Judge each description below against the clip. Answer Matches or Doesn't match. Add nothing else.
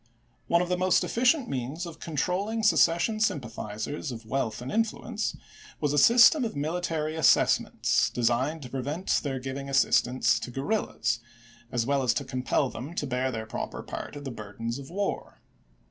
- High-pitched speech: Doesn't match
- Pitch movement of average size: Doesn't match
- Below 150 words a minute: Doesn't match